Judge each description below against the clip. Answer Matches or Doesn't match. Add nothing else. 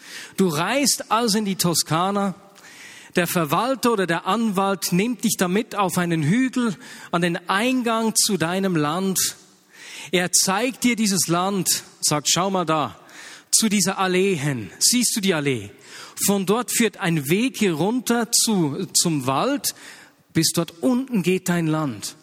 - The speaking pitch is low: Doesn't match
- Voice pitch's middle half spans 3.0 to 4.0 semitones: Doesn't match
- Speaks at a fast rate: Doesn't match